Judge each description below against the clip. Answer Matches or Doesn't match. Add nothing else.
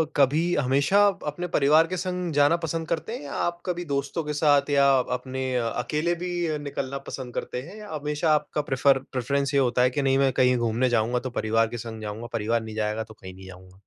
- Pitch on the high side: Doesn't match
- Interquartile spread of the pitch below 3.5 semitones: Doesn't match